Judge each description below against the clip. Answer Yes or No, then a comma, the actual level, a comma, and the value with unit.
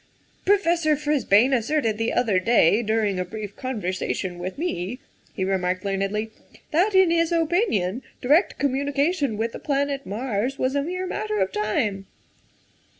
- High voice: Yes, high, 235 Hz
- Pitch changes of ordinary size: No, wide, 6.8 semitones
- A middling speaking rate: Yes, average, 150 wpm